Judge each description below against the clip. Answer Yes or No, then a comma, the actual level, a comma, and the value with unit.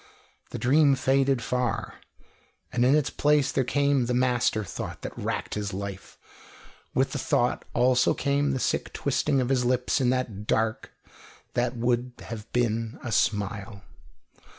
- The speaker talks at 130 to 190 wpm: Yes, average, 150 wpm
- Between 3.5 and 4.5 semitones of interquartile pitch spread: No, average, 2.9 semitones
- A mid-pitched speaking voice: No, low, 125 Hz